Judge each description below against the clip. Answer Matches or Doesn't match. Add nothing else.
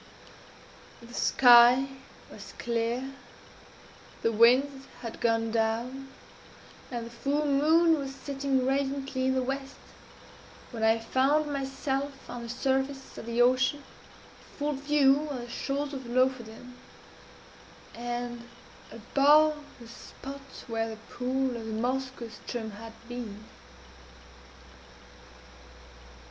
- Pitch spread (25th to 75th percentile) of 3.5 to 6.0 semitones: Doesn't match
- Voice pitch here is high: Matches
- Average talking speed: Doesn't match